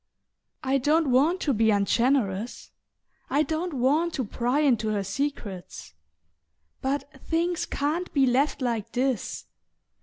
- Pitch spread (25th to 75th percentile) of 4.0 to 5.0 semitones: Yes, average, 4.5 semitones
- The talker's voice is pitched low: No, very high, 265 Hz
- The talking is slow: Yes, slow, 125 wpm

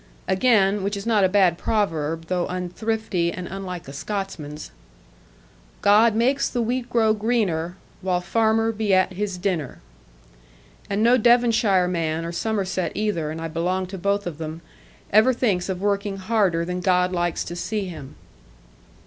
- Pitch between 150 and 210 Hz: Yes, high, 190 Hz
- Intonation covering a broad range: No, average, 3.7 semitones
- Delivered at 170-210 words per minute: No, average, 160 wpm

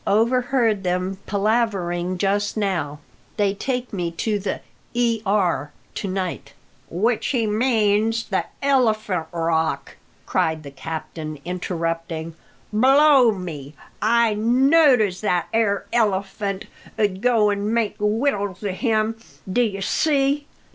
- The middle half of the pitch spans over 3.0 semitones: Yes, average, 4.2 semitones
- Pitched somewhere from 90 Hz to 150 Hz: No, high, 205 Hz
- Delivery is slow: Yes, slow, 120 wpm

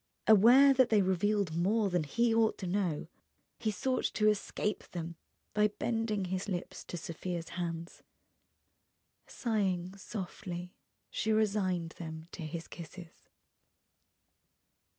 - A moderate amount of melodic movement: Yes, average, 3.8 semitones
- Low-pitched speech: No, high, 190 Hz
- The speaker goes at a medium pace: No, slow, 120 wpm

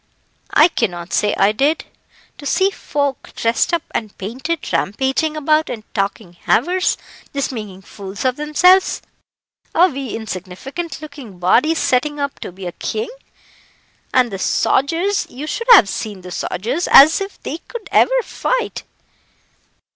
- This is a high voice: Yes, very high, 270 Hz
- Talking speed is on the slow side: No, average, 145 wpm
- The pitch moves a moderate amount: No, wide, 7.8 semitones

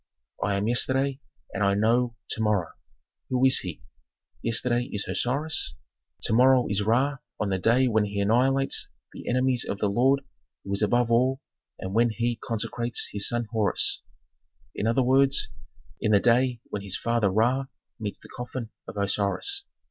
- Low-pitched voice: Yes, low, 115 Hz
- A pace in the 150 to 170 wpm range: Yes, average, 165 wpm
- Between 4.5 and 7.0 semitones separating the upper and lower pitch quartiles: No, average, 3.7 semitones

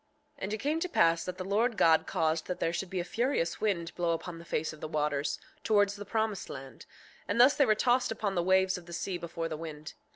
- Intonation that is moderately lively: Yes, average, 4.4 semitones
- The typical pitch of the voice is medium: Yes, medium, 180 Hz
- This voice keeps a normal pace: No, fast, 255 wpm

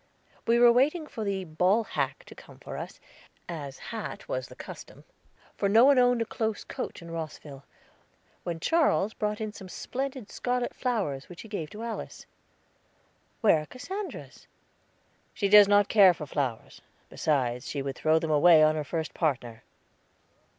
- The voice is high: Yes, high, 195 Hz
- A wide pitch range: Yes, wide, 6.8 semitones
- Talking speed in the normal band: Yes, average, 165 wpm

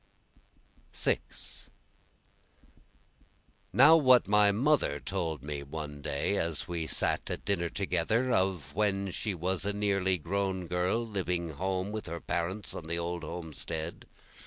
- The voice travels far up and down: No, average, 3.5 semitones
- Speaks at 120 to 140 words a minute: Yes, slow, 135 wpm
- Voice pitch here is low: Yes, very low, 90 Hz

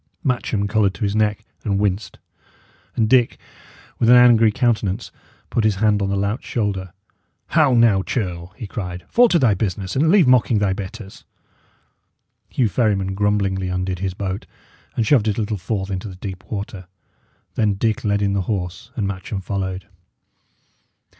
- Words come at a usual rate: Yes, average, 165 wpm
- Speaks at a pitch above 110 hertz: No, low, 100 Hz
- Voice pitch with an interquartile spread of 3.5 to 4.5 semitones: No, average, 2.8 semitones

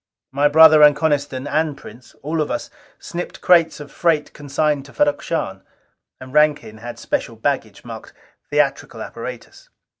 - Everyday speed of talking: Yes, average, 150 wpm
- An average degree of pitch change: No, narrow, 2.3 semitones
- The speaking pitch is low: No, medium, 150 Hz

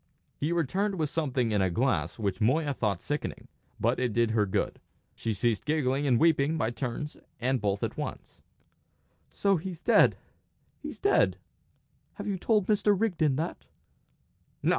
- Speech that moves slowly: No, average, 155 wpm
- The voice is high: No, medium, 140 Hz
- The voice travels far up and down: Yes, wide, 6.4 semitones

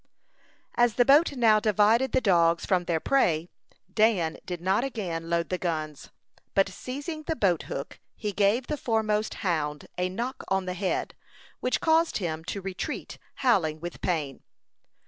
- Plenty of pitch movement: Yes, wide, 5.8 semitones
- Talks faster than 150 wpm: Yes, average, 160 wpm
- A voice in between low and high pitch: No, high, 195 Hz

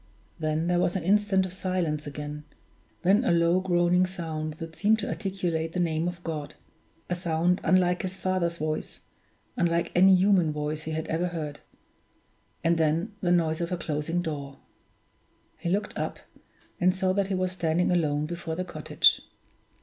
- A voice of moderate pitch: Yes, medium, 175 Hz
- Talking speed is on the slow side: No, average, 170 wpm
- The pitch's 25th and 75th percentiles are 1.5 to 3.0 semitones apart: Yes, narrow, 2.5 semitones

